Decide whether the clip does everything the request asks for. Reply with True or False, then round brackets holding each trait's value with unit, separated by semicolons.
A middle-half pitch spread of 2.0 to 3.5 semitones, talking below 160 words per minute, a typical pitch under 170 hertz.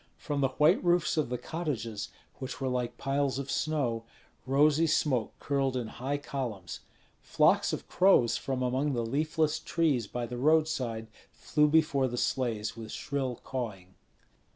False (3.9 semitones; 150 wpm; 135 Hz)